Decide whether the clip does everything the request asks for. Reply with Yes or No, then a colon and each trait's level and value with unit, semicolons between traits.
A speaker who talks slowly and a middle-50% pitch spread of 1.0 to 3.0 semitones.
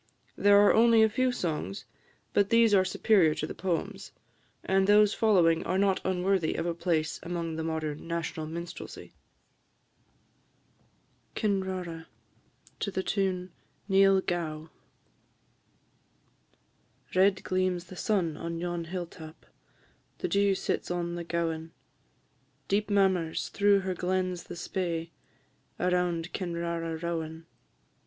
Yes: slow, 120 wpm; average, 2.7 semitones